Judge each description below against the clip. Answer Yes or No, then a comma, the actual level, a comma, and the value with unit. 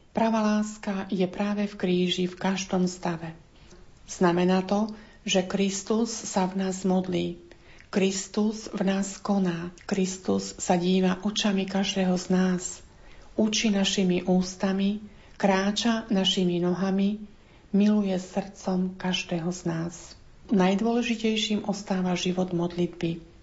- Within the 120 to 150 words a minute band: No, slow, 110 wpm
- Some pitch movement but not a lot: No, narrow, 2.1 semitones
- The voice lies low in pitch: No, high, 190 Hz